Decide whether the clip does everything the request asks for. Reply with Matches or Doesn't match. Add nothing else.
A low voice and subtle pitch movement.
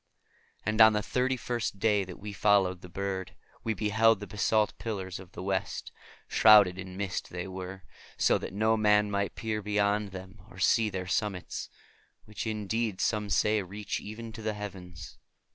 Matches